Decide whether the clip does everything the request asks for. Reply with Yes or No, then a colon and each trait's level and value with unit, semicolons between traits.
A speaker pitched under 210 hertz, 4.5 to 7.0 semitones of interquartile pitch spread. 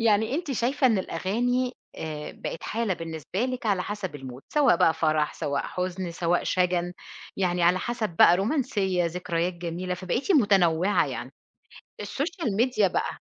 Yes: medium, 185 Hz; average, 5.3 semitones